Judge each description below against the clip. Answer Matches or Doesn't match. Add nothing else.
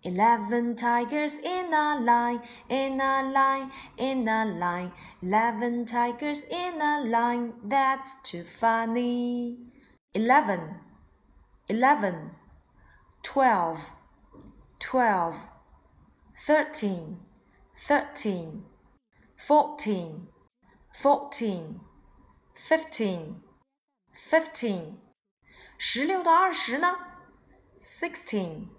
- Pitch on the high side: Matches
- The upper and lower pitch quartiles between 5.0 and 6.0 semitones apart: Matches